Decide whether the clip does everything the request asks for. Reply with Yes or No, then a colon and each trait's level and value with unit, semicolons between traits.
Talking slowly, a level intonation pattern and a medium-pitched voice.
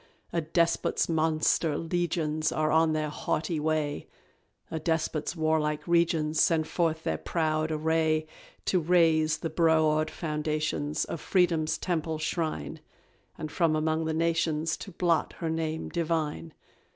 Yes: slow, 130 wpm; narrow, 1.2 semitones; medium, 160 Hz